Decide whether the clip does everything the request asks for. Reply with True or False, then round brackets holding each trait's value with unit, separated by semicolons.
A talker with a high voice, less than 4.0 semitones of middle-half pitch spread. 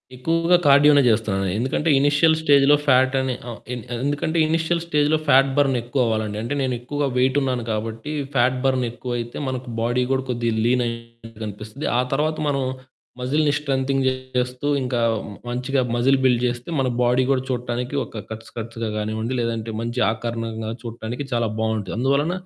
False (125 Hz; 3.0 semitones)